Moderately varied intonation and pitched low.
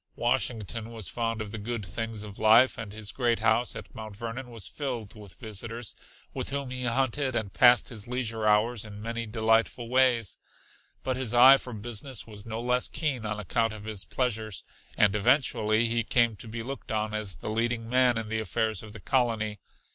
No: narrow, 2.2 semitones; low, 115 Hz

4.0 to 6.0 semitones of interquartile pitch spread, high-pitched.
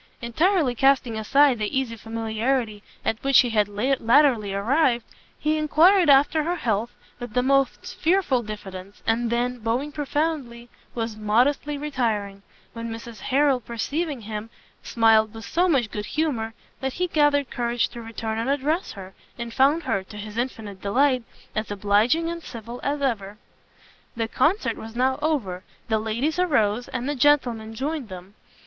Yes: average, 4.6 semitones; high, 240 Hz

